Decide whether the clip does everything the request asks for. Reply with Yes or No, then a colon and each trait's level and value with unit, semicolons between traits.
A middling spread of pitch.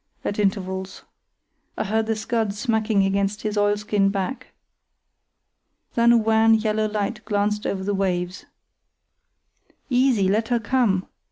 No: narrow, 2.1 semitones